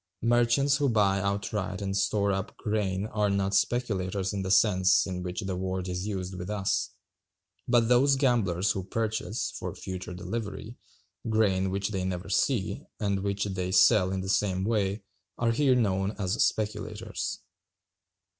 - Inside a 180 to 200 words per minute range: No, average, 155 wpm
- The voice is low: Yes, low, 100 Hz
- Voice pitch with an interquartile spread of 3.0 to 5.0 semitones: No, narrow, 2.6 semitones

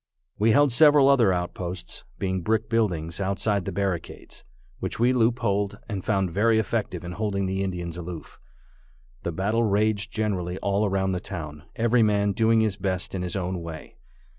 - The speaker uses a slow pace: No, average, 165 wpm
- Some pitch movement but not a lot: Yes, average, 3.4 semitones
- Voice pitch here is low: Yes, low, 100 Hz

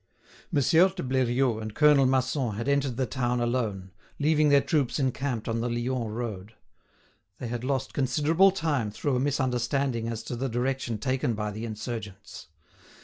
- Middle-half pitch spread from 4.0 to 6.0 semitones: No, average, 3.2 semitones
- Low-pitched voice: Yes, low, 125 Hz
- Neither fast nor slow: Yes, average, 160 wpm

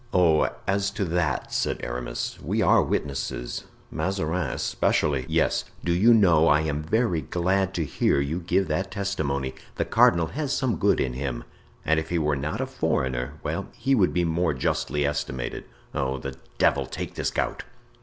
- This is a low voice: Yes, very low, 80 Hz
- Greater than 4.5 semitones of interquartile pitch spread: Yes, average, 5.3 semitones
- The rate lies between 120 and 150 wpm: No, average, 170 wpm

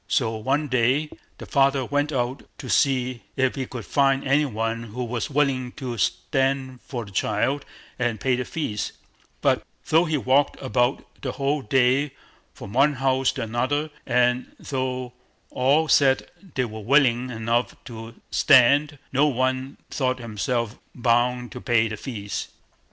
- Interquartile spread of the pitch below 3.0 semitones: Yes, narrow, 2.4 semitones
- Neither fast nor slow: Yes, average, 155 wpm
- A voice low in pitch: Yes, low, 130 Hz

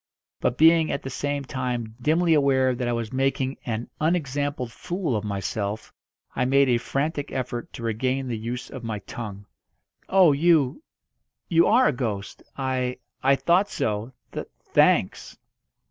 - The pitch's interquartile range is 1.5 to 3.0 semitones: No, average, 3.7 semitones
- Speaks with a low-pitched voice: Yes, low, 130 Hz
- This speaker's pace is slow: No, average, 155 wpm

